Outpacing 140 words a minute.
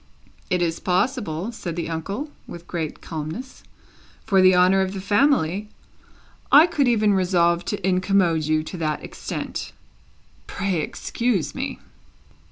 No: slow, 135 wpm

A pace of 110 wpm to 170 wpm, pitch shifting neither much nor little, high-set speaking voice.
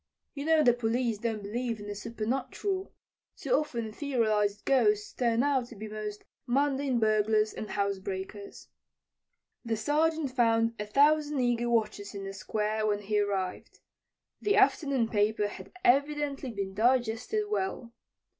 Yes: average, 140 wpm; average, 4.4 semitones; high, 230 Hz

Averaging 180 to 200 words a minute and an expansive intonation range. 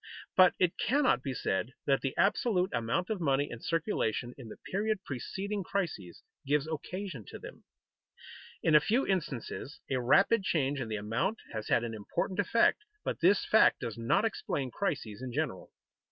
No: average, 170 wpm; wide, 8.2 semitones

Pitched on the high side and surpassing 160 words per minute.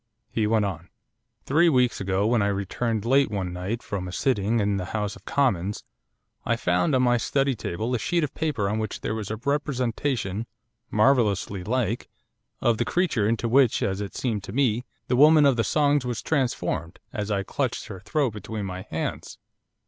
No: low, 110 Hz; average, 190 wpm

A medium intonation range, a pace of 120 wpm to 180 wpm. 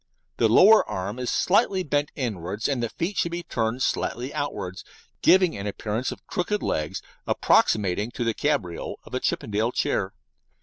No: wide, 6.8 semitones; average, 165 wpm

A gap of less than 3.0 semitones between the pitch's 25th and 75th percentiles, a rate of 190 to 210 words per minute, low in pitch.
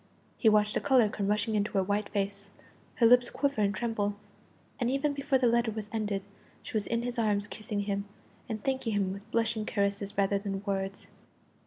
No: narrow, 2.6 semitones; average, 195 wpm; high, 210 Hz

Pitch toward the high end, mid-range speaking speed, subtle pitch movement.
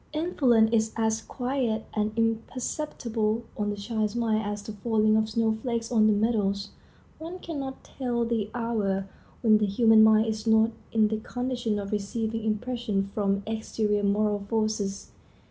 Yes: high, 220 Hz; average, 155 wpm; narrow, 1.8 semitones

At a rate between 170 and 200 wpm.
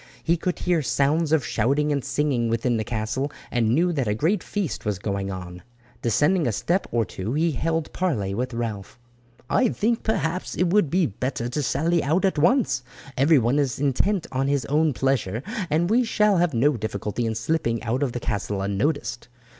Yes: average, 190 wpm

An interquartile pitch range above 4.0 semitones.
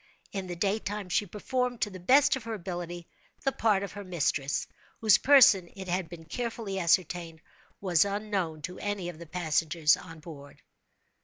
No: average, 3.6 semitones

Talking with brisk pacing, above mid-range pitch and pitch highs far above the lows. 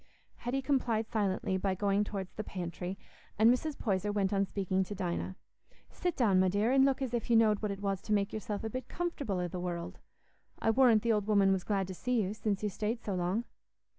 No: fast, 225 wpm; high, 205 Hz; average, 3.2 semitones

